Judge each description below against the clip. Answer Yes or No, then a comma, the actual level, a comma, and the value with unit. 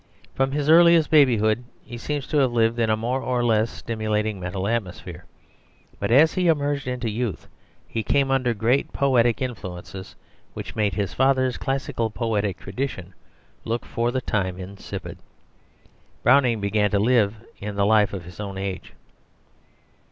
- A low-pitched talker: Yes, low, 115 Hz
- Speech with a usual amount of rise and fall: Yes, average, 4.3 semitones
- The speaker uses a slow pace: No, average, 155 wpm